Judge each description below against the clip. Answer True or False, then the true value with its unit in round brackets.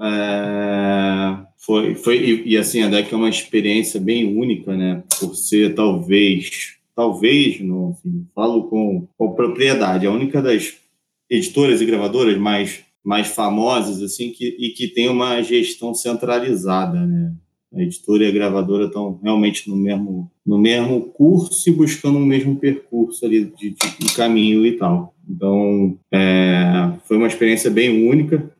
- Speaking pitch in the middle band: False (110 Hz)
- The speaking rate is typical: True (155 wpm)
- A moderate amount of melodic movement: True (3.5 semitones)